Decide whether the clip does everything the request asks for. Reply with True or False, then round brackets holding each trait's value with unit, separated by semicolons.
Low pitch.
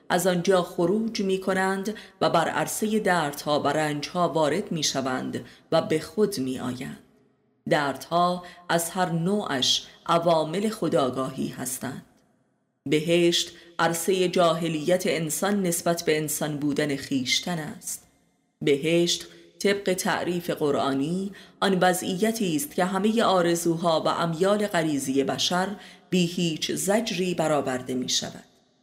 False (170 Hz)